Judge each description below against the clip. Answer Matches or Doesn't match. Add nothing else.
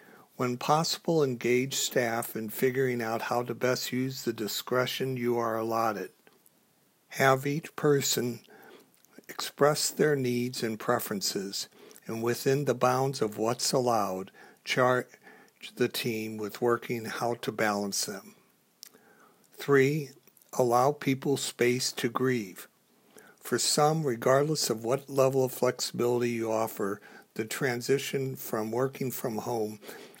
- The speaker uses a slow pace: Matches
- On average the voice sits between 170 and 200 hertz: Doesn't match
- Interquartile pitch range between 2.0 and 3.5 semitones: Matches